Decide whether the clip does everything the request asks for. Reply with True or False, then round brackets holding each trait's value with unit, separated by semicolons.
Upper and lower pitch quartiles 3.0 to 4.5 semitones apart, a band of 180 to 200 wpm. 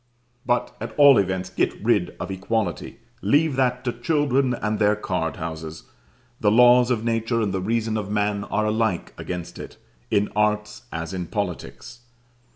False (3.7 semitones; 165 wpm)